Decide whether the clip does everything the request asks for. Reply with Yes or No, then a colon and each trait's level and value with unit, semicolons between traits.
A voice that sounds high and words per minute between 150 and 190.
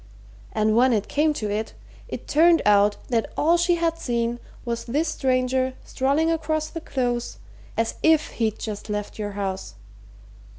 Yes: very high, 250 Hz; average, 160 wpm